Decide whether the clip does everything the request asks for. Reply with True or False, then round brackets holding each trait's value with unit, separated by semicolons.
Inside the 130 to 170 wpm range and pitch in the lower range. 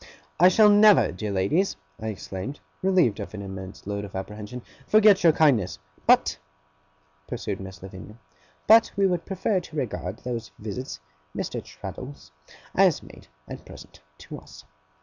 True (150 wpm; 120 Hz)